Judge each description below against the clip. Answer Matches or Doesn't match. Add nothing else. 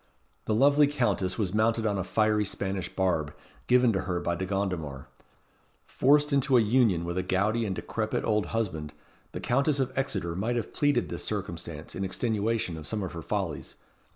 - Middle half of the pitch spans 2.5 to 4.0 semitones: Doesn't match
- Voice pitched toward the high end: Doesn't match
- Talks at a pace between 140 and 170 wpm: Doesn't match